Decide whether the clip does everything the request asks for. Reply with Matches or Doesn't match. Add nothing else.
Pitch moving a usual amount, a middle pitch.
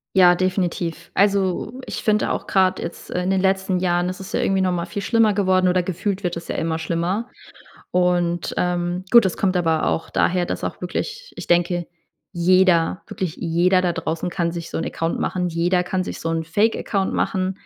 Doesn't match